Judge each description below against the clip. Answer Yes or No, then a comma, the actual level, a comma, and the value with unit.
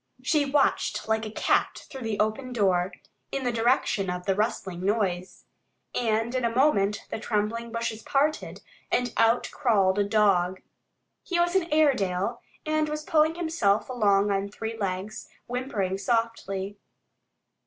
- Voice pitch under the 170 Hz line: No, high, 225 Hz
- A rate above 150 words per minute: No, average, 145 wpm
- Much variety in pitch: No, average, 4.5 semitones